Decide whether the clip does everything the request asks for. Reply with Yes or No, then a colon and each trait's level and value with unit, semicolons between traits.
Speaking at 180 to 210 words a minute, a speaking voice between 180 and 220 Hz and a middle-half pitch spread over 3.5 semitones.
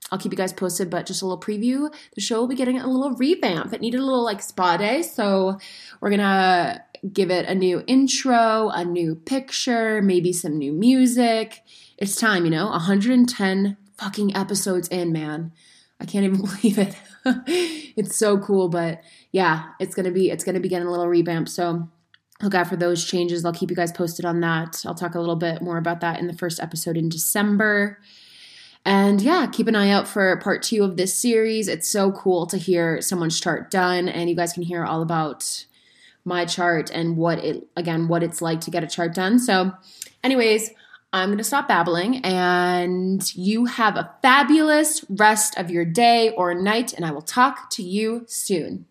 Yes: average, 200 wpm; high, 190 Hz; average, 4.1 semitones